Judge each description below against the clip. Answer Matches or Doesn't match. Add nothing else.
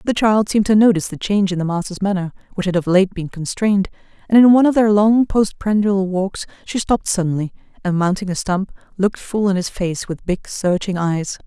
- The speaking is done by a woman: Matches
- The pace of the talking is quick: Matches